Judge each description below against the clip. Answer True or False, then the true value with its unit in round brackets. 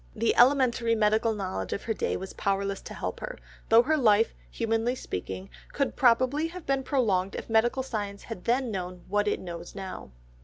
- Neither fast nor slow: True (185 wpm)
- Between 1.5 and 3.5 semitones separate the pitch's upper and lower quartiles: False (4.2 semitones)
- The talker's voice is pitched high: True (225 Hz)